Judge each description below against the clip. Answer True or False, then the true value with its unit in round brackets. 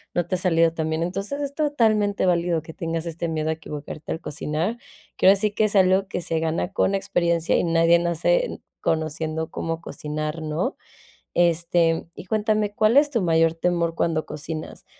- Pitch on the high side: False (170 Hz)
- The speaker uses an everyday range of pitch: True (3.5 semitones)